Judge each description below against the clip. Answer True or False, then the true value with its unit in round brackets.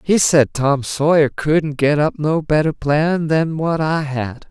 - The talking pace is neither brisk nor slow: True (185 wpm)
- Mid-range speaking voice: True (150 Hz)